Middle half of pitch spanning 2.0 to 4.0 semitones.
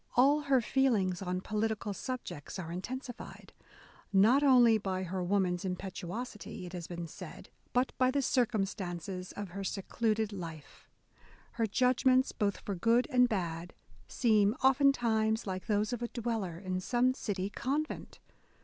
No: average, 5.0 semitones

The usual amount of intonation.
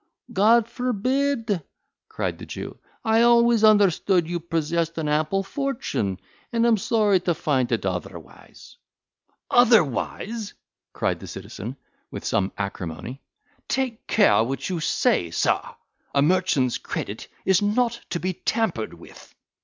No: wide, 7.6 semitones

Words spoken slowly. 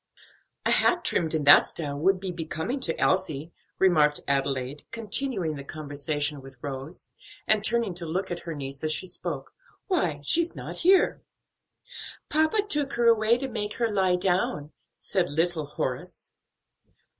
No: average, 155 wpm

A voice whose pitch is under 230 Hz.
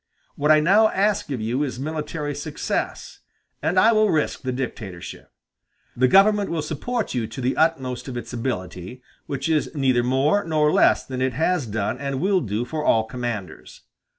Yes: medium, 140 Hz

